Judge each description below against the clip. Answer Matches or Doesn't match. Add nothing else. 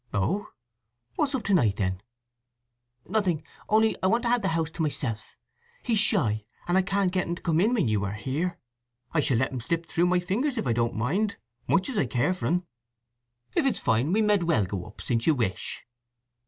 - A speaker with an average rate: Doesn't match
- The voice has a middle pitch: Matches